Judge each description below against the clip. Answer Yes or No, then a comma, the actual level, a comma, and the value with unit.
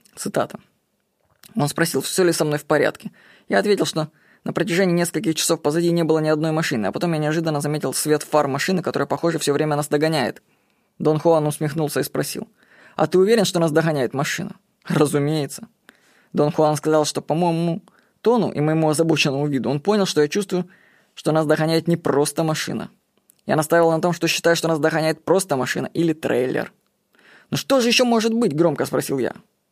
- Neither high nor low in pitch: Yes, medium, 160 Hz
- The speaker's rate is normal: No, fast, 190 wpm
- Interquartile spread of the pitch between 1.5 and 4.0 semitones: Yes, average, 2.9 semitones